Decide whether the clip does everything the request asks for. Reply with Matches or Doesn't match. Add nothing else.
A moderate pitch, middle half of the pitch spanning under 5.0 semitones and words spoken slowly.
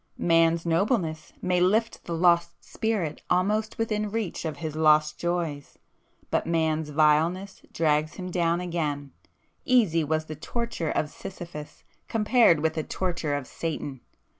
Matches